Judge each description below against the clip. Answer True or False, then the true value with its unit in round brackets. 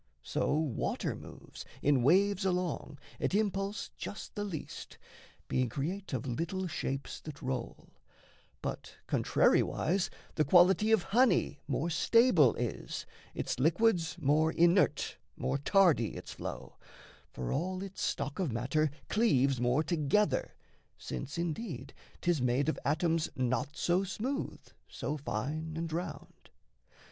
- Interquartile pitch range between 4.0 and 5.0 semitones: False (5.5 semitones)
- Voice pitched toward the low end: False (160 Hz)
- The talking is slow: True (125 wpm)